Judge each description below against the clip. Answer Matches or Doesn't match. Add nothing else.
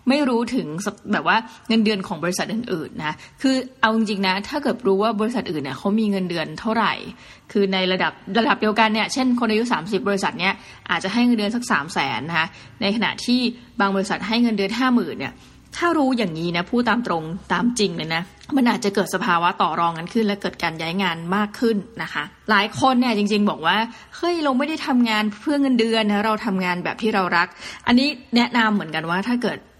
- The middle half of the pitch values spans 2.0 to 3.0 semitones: Doesn't match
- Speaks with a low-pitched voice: Doesn't match